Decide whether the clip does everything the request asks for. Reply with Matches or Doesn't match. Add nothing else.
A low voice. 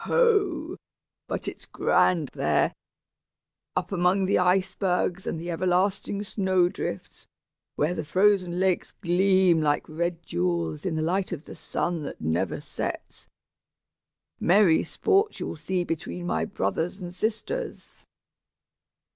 Doesn't match